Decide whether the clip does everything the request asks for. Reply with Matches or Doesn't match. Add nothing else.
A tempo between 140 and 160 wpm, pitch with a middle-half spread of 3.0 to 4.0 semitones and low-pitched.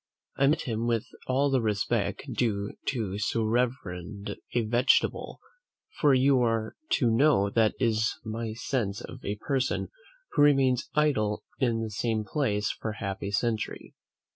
Matches